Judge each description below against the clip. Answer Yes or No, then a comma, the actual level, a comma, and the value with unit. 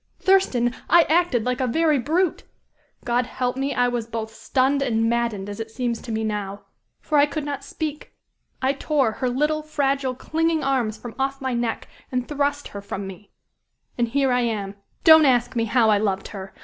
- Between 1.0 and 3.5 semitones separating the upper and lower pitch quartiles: No, average, 4.1 semitones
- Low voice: No, very high, 250 Hz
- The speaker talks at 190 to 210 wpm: Yes, average, 195 wpm